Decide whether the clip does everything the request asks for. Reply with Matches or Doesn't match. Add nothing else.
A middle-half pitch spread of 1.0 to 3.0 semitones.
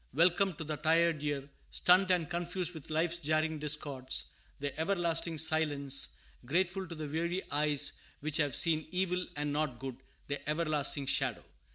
Matches